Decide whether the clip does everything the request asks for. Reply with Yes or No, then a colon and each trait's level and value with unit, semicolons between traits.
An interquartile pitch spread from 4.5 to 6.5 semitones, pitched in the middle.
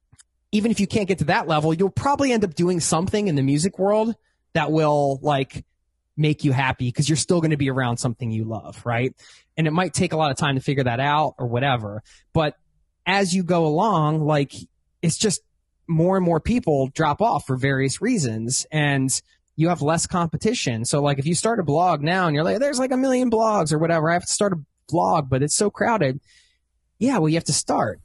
Yes: average, 5.2 semitones; medium, 155 Hz